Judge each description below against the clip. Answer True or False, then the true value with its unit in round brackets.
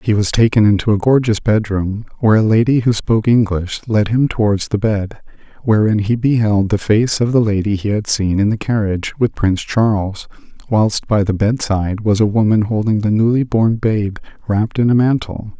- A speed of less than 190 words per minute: False (195 wpm)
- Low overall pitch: True (110 Hz)